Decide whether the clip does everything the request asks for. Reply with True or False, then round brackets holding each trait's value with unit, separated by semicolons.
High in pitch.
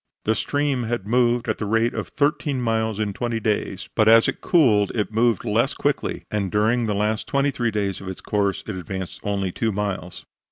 False (110 Hz)